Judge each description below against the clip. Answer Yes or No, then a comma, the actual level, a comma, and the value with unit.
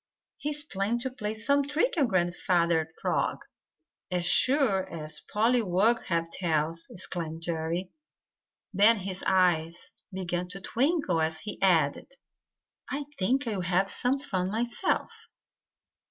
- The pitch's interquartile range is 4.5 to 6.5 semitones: Yes, wide, 5.6 semitones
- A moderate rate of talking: No, slow, 125 wpm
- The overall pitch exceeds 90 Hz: Yes, high, 190 Hz